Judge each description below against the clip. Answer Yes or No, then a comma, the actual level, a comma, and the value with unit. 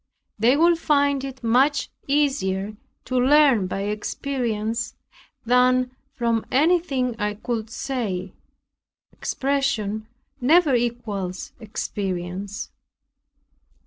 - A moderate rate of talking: No, slow, 85 wpm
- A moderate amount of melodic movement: Yes, average, 4.7 semitones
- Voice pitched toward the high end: Yes, high, 240 Hz